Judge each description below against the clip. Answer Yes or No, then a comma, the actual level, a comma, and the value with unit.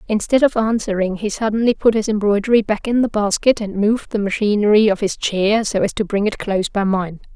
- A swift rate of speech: Yes, fast, 220 wpm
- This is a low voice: No, high, 210 Hz